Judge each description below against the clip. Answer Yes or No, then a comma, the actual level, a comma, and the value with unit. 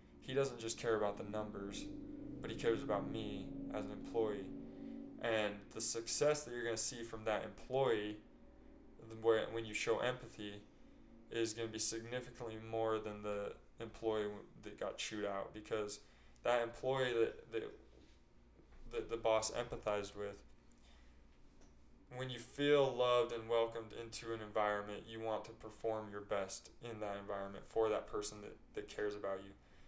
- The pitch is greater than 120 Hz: No, low, 110 Hz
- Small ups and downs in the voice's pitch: Yes, narrow, 2.2 semitones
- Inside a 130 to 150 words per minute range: No, average, 160 wpm